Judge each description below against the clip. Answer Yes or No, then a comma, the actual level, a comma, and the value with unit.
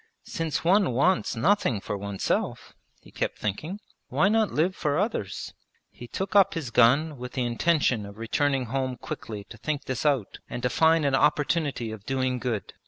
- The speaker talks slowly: No, average, 175 wpm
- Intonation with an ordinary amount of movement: No, wide, 5.8 semitones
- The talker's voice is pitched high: No, low, 135 Hz